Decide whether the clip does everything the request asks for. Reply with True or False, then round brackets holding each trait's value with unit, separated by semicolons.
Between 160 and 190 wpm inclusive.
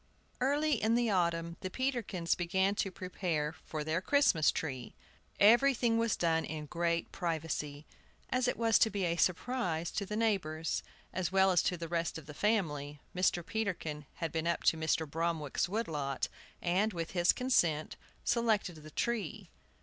True (165 wpm)